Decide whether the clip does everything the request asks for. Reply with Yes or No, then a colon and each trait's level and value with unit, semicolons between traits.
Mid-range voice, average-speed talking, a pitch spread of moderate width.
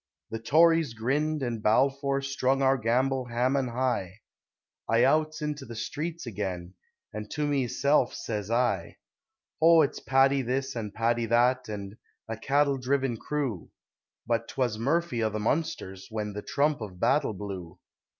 No: low, 125 Hz; average, 150 wpm; average, 4.1 semitones